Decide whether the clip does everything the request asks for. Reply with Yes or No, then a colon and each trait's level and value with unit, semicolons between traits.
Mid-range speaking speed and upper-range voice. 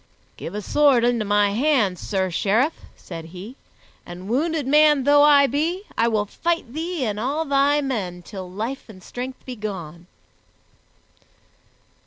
Yes: average, 150 wpm; high, 240 Hz